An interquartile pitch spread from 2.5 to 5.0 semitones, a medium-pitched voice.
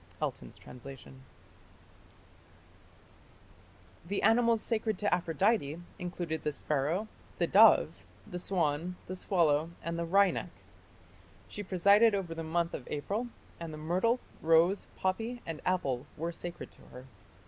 Yes: average, 4.1 semitones; medium, 175 Hz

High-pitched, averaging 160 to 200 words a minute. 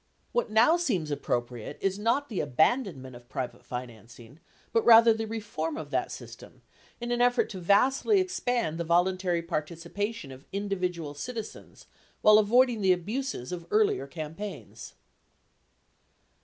No: high, 195 Hz; average, 140 wpm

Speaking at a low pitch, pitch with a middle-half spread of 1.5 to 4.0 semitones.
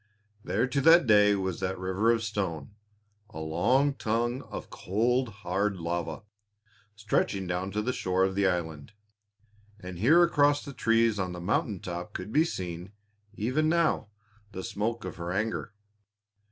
No: low, 105 Hz; average, 4.4 semitones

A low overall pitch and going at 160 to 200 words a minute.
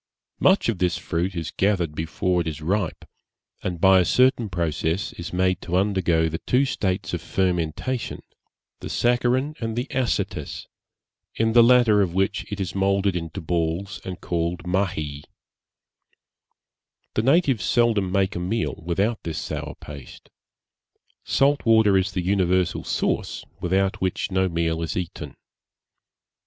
No: very low, 95 Hz; average, 145 wpm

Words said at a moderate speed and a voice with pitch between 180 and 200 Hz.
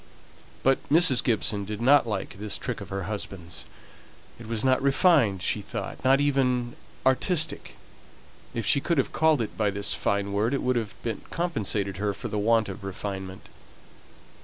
No: average, 165 wpm; low, 115 Hz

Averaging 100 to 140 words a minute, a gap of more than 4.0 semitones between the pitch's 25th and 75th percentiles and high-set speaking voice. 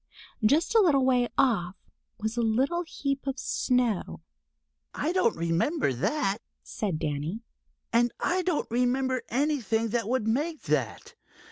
Yes: slow, 135 wpm; average, 4.7 semitones; very high, 250 Hz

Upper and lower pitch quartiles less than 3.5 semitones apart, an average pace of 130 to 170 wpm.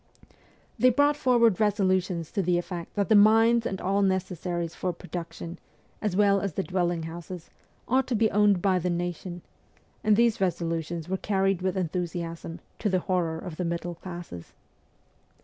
Yes: average, 2.9 semitones; average, 165 wpm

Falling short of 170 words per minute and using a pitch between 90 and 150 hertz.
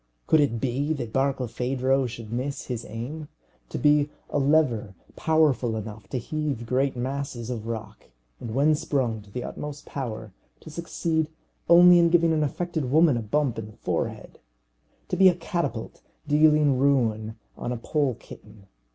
Yes: average, 160 wpm; low, 135 Hz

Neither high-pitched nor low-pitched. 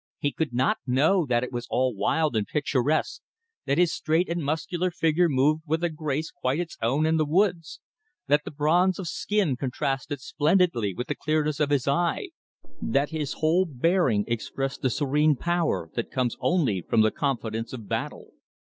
Yes: medium, 150 Hz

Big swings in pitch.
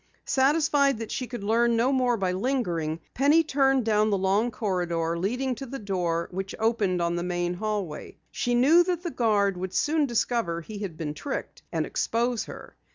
Yes: wide, 6.0 semitones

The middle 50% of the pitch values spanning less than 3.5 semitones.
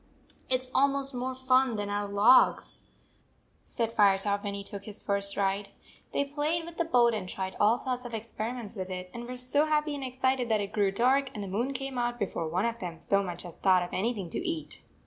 No: average, 4.6 semitones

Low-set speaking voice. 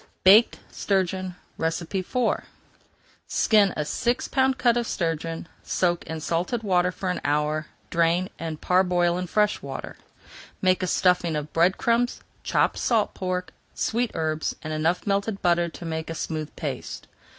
No: medium, 180 Hz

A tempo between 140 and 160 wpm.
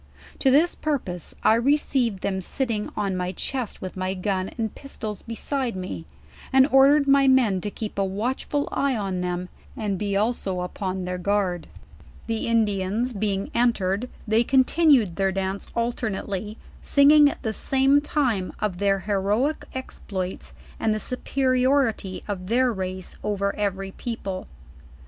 Yes: average, 150 wpm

